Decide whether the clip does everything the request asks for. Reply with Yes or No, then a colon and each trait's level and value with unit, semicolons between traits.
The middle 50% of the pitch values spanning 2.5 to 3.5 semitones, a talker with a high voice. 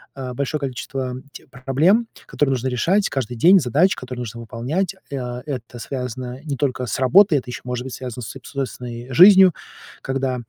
No: average, 2.9 semitones; low, 130 Hz